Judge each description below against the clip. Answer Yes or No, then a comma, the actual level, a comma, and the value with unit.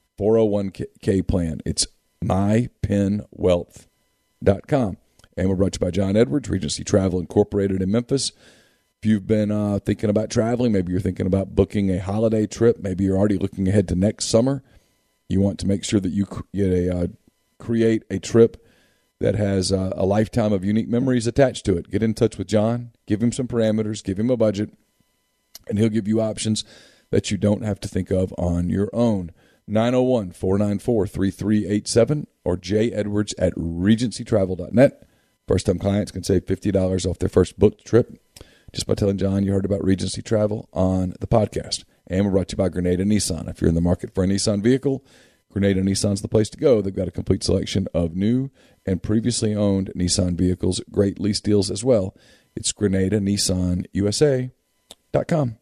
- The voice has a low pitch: Yes, low, 100 Hz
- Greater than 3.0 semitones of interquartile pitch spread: No, average, 2.7 semitones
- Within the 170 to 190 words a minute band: Yes, average, 180 wpm